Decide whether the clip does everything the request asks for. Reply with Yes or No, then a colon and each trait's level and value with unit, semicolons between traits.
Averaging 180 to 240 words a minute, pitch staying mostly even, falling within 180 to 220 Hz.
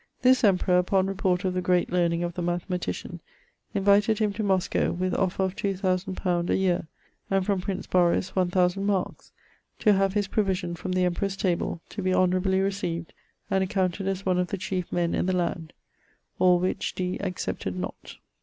Yes: average, 185 wpm; narrow, 1.6 semitones; medium, 185 Hz